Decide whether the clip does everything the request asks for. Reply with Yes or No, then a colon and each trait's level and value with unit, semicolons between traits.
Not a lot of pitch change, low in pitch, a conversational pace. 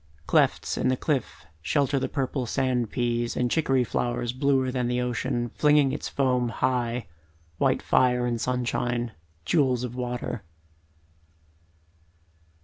No: narrow, 1.5 semitones; low, 125 Hz; slow, 130 wpm